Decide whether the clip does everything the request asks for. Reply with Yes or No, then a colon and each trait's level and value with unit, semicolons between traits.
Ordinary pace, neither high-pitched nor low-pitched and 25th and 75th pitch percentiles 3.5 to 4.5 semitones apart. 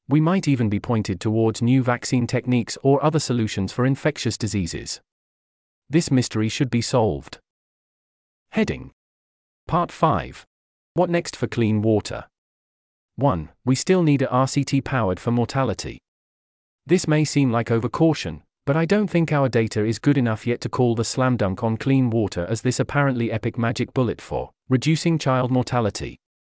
No: average, 160 wpm; low, 120 Hz; average, 4.1 semitones